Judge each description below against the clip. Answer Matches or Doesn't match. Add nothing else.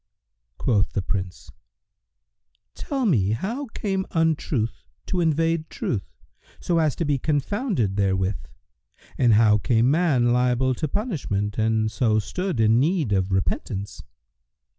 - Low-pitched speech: Matches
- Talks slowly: Matches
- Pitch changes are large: Matches